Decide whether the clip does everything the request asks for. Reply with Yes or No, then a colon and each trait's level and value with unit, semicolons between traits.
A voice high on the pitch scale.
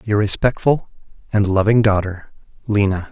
No: low, 105 Hz